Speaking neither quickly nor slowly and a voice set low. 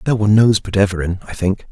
No: fast, 245 wpm; low, 100 Hz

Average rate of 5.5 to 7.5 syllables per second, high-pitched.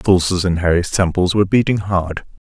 No: 5.8 syllables/s; very low, 95 Hz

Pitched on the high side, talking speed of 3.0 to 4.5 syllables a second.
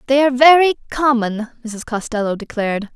No: high, 245 Hz; 5.5 syllables/s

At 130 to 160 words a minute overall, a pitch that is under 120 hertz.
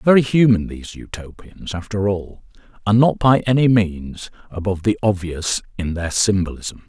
Yes: average, 150 wpm; low, 100 Hz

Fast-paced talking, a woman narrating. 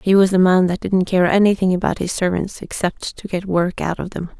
Yes: fast, 245 wpm; female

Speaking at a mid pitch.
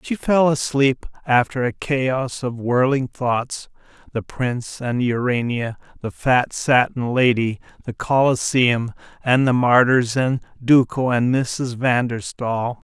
No: low, 125 Hz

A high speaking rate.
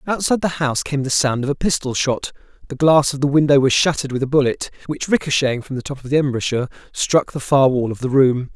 Yes: fast, 245 wpm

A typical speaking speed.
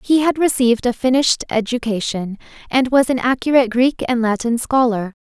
Yes: average, 160 wpm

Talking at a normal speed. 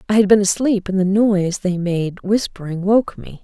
No: fast, 210 wpm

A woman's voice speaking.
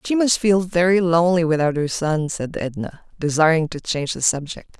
Yes: female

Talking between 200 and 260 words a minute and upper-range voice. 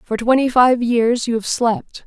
Yes: fast, 205 wpm; high, 240 Hz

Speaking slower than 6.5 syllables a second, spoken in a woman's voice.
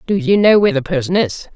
No: 6.6 syllables/s; female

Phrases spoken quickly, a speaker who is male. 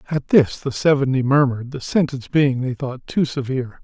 No: average, 190 wpm; male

